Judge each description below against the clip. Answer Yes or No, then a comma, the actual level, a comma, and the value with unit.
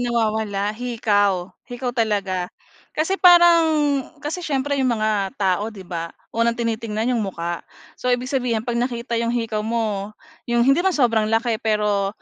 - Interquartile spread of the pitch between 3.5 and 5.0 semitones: No, average, 3.0 semitones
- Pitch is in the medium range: No, high, 225 Hz